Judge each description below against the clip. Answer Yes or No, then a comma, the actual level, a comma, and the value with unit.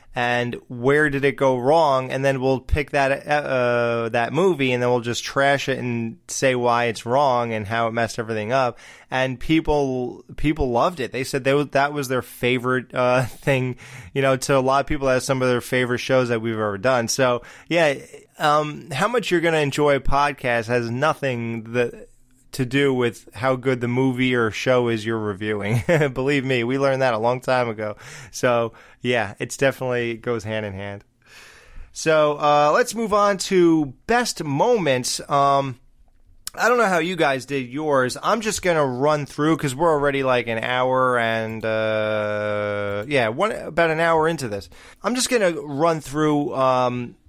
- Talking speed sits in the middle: Yes, average, 190 wpm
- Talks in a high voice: No, low, 130 Hz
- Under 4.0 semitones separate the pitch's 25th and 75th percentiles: Yes, average, 3.3 semitones